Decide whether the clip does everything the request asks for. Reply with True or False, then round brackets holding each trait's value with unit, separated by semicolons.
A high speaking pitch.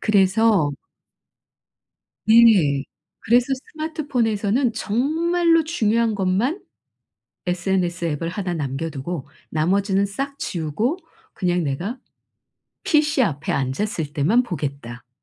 True (200 Hz)